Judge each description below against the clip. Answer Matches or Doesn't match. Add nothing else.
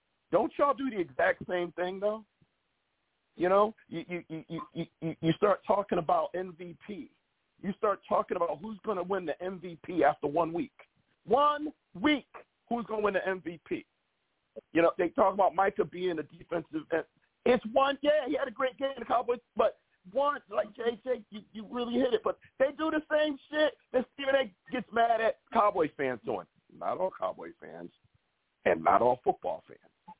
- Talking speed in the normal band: Matches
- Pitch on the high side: Matches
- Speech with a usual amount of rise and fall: Doesn't match